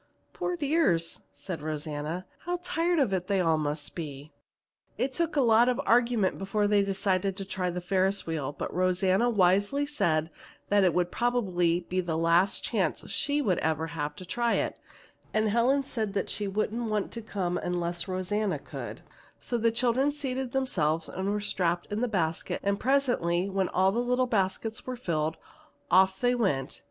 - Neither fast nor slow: Yes, average, 180 wpm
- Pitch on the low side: No, high, 195 Hz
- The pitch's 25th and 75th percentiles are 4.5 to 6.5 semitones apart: Yes, wide, 5.5 semitones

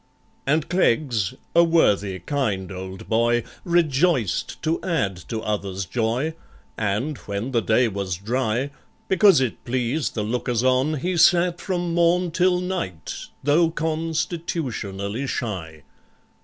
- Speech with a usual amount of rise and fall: No, wide, 7.8 semitones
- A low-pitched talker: Yes, low, 130 Hz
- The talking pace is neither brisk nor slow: No, slow, 120 wpm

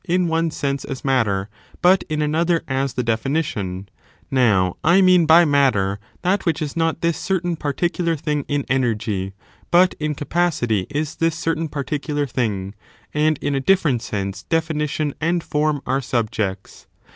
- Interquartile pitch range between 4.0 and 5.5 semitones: Yes, average, 5.2 semitones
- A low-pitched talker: No, medium, 145 Hz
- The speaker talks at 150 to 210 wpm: Yes, average, 165 wpm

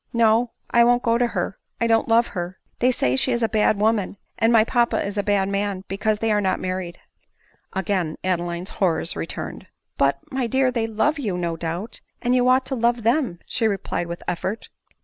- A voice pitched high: Yes, high, 215 Hz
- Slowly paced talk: No, fast, 205 wpm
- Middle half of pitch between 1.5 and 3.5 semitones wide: No, average, 4.3 semitones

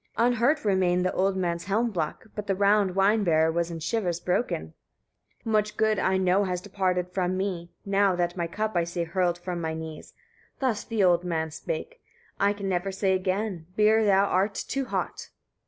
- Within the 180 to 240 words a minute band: Yes, average, 190 wpm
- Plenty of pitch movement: No, average, 2.9 semitones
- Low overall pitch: No, high, 190 Hz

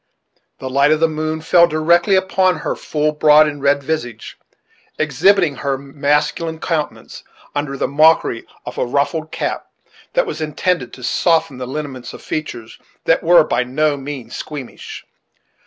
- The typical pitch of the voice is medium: Yes, medium, 150 Hz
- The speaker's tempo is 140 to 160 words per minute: Yes, average, 155 wpm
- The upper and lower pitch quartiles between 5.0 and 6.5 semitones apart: No, average, 2.7 semitones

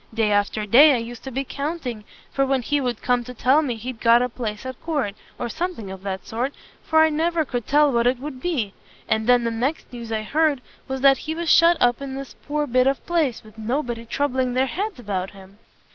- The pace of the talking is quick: Yes, fast, 235 wpm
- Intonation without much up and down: No, average, 4.1 semitones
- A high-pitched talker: Yes, very high, 255 Hz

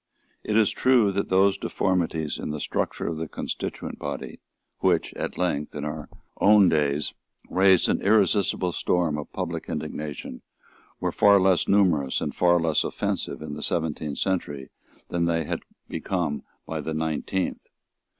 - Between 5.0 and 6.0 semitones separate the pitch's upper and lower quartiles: No, average, 4.0 semitones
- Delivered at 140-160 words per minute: Yes, average, 150 wpm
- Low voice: Yes, very low, 85 Hz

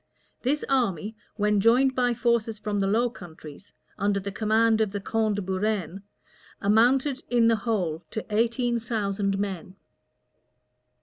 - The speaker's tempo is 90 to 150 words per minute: Yes, average, 140 wpm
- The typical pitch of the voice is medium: No, high, 215 Hz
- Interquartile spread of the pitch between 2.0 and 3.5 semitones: Yes, average, 2.9 semitones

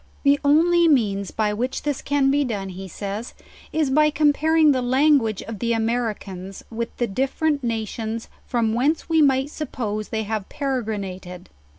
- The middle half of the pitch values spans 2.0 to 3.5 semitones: No, average, 5.1 semitones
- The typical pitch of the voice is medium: No, high, 240 Hz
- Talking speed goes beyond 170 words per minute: No, average, 165 wpm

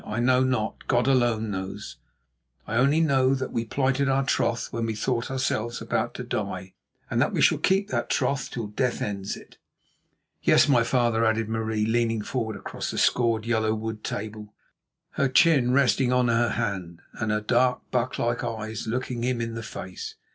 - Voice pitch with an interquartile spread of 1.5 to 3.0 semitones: Yes, average, 2.7 semitones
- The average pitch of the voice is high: No, low, 115 Hz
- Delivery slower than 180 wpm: No, average, 185 wpm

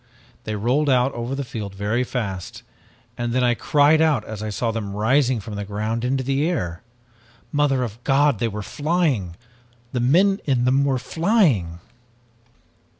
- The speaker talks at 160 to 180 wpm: Yes, average, 165 wpm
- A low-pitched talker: Yes, low, 125 Hz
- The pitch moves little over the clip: No, average, 4.7 semitones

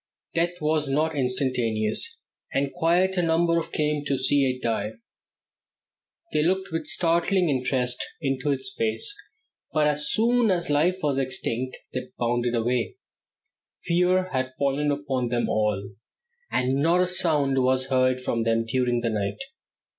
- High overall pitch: No, medium, 140 Hz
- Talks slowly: No, average, 145 wpm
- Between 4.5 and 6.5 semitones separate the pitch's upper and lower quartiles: Yes, average, 4.8 semitones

